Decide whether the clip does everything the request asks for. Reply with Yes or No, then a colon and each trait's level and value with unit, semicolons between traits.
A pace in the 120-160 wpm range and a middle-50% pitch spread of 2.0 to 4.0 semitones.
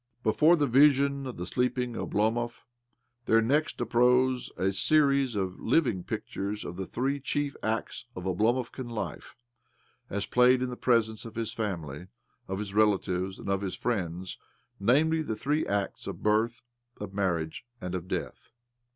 No: average, 155 wpm; average, 4.8 semitones